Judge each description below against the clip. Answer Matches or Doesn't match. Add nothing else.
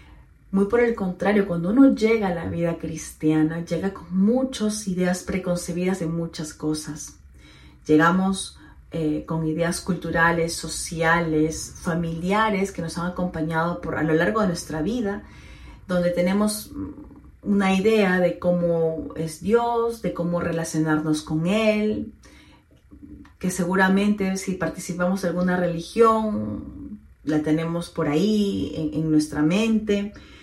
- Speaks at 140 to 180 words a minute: Doesn't match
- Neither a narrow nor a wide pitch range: Matches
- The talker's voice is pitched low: Doesn't match